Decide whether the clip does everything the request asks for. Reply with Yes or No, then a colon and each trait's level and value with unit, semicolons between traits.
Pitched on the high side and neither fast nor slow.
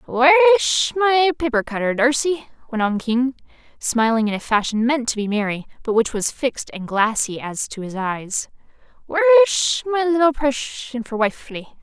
Yes: very high, 255 Hz; average, 160 wpm